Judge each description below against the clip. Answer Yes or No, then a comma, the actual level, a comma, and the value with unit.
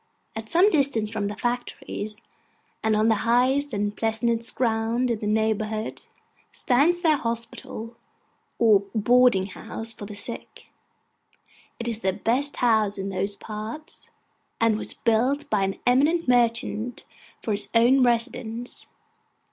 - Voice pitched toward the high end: Yes, high, 230 Hz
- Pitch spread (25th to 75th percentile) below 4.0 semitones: Yes, narrow, 2.5 semitones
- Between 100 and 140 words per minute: Yes, slow, 135 wpm